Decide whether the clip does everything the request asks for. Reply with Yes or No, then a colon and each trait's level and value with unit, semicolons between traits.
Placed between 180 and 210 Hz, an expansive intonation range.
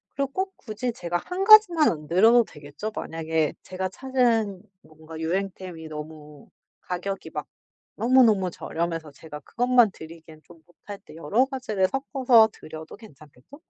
Yes: medium, 185 Hz; wide, 7.3 semitones